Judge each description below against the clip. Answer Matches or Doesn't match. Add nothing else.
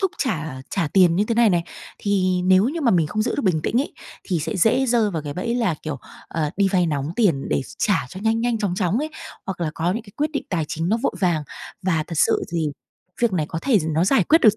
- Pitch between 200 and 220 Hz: Doesn't match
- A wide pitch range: Matches